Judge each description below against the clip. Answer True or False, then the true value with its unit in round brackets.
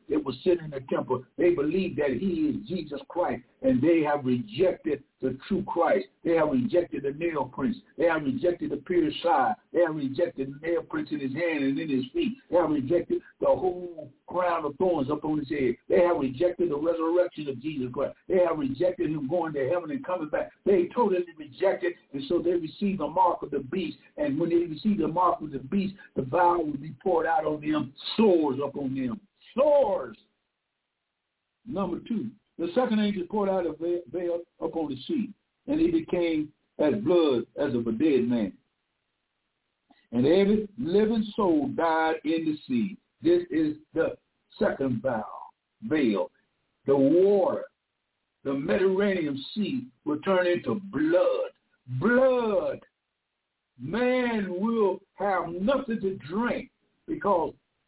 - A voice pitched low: False (180 Hz)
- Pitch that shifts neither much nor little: False (7.0 semitones)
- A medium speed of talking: True (165 wpm)